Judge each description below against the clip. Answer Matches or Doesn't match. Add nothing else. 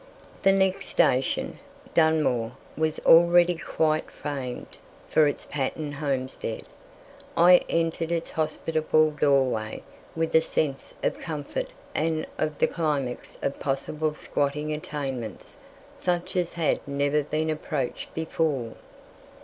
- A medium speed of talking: Doesn't match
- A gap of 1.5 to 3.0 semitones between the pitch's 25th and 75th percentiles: Matches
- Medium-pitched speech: Matches